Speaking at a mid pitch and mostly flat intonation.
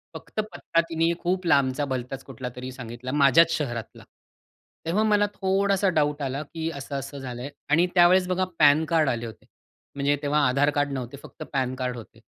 No: medium, 145 Hz; average, 4.4 semitones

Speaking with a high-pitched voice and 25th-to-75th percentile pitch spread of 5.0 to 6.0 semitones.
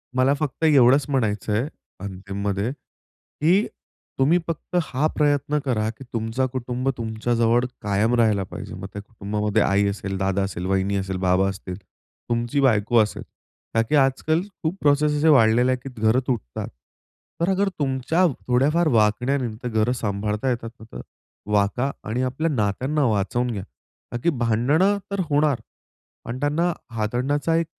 No: low, 120 Hz; average, 5.3 semitones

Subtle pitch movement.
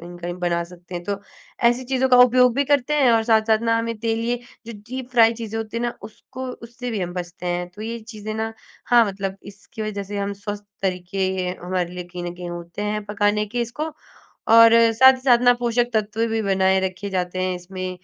No: average, 4.1 semitones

